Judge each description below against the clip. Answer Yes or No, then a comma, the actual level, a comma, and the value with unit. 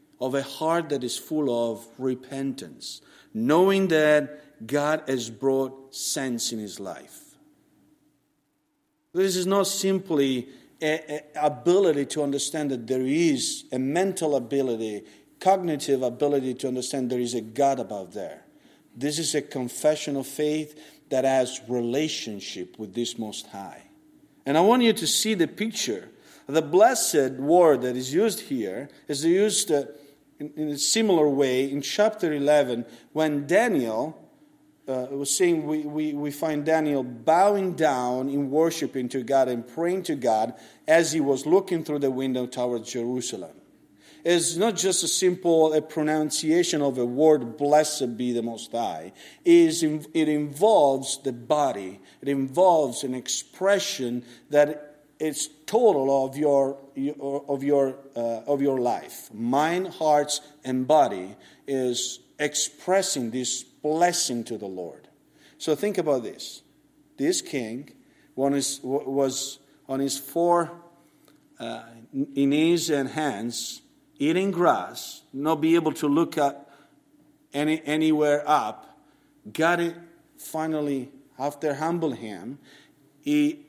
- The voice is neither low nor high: Yes, medium, 145 Hz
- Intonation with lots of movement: No, average, 4.0 semitones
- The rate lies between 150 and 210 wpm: No, slow, 135 wpm